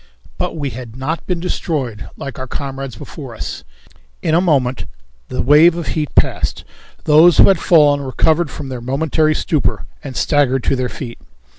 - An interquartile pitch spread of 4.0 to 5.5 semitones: No, average, 3.5 semitones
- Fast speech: No, average, 170 wpm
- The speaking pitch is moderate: Yes, medium, 145 Hz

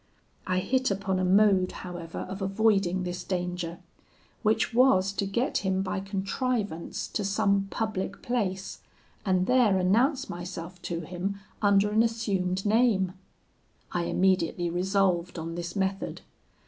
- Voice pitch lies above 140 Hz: Yes, high, 190 Hz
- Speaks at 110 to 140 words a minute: Yes, slow, 135 wpm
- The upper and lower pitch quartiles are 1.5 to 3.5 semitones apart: Yes, narrow, 2.5 semitones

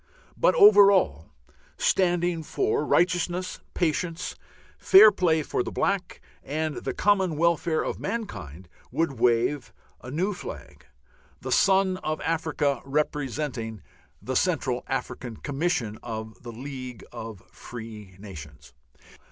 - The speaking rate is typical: No, slow, 120 wpm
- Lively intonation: Yes, wide, 7.5 semitones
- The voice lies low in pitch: No, medium, 150 Hz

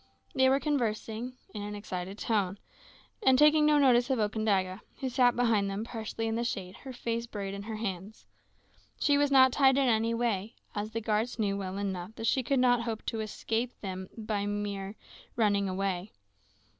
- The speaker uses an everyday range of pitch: Yes, average, 3.5 semitones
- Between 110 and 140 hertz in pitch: No, high, 220 Hz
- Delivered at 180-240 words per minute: Yes, average, 190 wpm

